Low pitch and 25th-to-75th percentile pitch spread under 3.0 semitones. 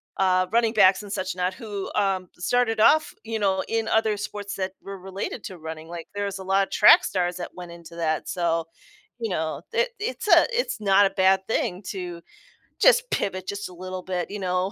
No: high, 190 Hz; narrow, 2.5 semitones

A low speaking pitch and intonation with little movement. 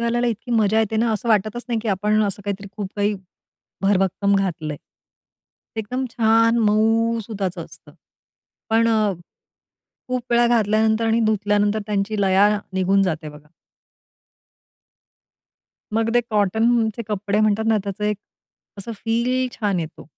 No: high, 215 Hz; narrow, 2.3 semitones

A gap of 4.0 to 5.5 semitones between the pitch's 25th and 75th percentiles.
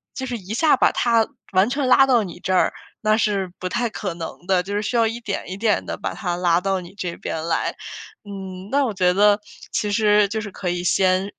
No: average, 3.3 semitones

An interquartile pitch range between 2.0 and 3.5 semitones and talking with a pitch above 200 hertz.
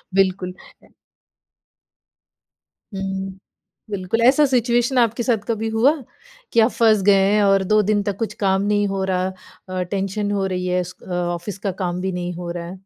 No: average, 3.0 semitones; high, 195 Hz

